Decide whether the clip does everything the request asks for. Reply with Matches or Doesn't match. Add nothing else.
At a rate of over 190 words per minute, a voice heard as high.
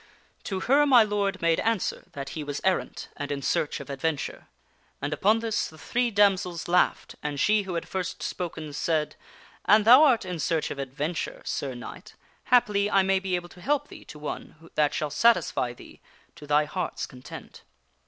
Doesn't match